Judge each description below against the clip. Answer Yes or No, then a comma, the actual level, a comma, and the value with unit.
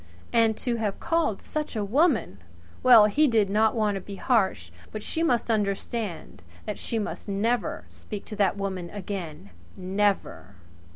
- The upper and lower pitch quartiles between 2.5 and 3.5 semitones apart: Yes, average, 2.9 semitones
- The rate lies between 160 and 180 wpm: Yes, average, 165 wpm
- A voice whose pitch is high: Yes, high, 210 Hz